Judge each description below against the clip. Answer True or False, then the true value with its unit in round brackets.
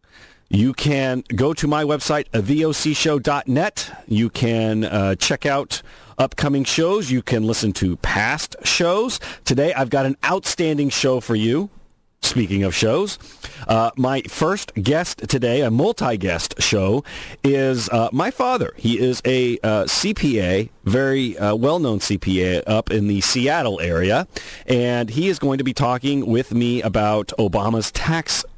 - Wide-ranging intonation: False (4.5 semitones)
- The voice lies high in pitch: False (125 Hz)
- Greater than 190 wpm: False (145 wpm)